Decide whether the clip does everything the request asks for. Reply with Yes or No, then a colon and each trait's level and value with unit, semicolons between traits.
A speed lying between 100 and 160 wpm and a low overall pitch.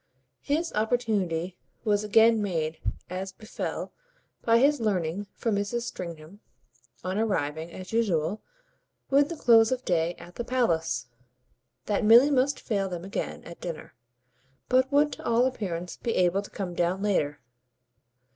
No: average, 145 wpm; high, 205 Hz